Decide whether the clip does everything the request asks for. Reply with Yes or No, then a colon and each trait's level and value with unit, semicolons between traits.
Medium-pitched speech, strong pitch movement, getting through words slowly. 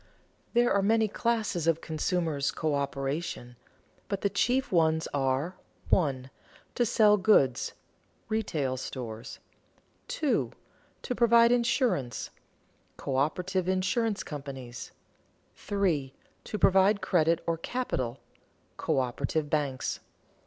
Yes: medium, 170 Hz; wide, 7.4 semitones; slow, 100 wpm